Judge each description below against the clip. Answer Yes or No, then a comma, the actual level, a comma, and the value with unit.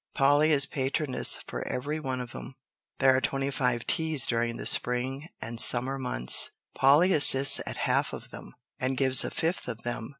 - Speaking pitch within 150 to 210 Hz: No, low, 130 Hz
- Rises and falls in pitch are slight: Yes, narrow, 2.3 semitones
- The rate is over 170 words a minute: Yes, average, 180 wpm